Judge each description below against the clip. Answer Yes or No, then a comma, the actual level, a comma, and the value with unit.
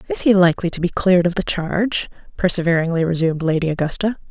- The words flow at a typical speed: Yes, average, 180 wpm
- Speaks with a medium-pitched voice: Yes, medium, 175 Hz